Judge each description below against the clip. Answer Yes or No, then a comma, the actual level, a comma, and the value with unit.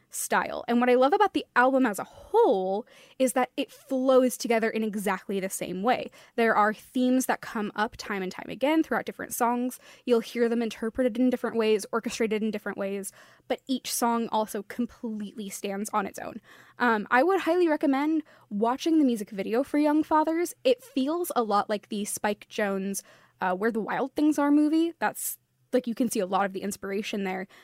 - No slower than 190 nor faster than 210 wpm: Yes, average, 200 wpm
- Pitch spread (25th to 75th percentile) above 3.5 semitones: Yes, average, 4.1 semitones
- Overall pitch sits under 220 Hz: No, high, 235 Hz